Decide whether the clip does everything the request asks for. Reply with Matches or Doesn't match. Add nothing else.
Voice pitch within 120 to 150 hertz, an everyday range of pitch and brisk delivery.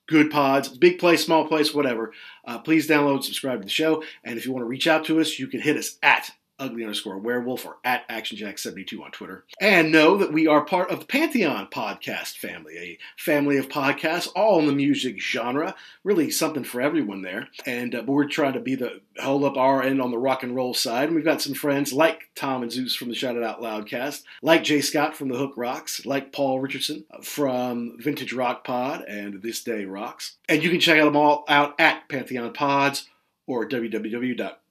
Matches